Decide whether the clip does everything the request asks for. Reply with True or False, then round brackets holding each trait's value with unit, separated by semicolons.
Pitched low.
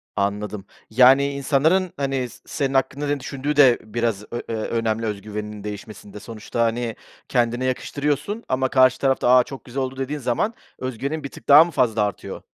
True (130 Hz)